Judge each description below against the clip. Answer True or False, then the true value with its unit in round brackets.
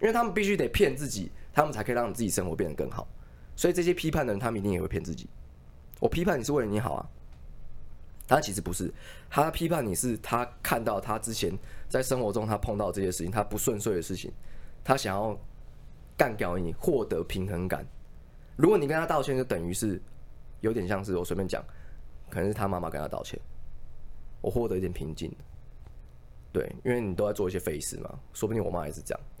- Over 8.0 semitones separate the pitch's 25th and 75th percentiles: True (9.0 semitones)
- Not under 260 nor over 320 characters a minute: True (315 characters per minute)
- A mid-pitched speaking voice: False (95 Hz)